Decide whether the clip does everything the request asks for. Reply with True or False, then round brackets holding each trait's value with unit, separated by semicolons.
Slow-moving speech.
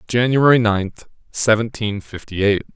True (110 wpm)